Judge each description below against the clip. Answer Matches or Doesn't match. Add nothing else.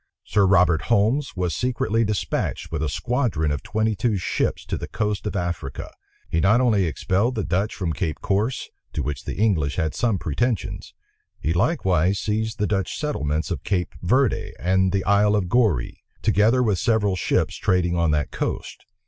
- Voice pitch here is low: Matches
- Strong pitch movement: Doesn't match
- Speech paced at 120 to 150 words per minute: Doesn't match